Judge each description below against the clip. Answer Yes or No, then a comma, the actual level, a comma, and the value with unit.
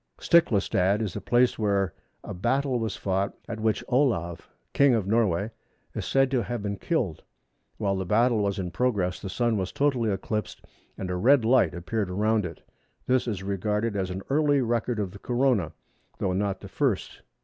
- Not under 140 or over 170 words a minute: No, average, 180 wpm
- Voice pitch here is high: No, low, 105 Hz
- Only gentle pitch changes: No, average, 4.1 semitones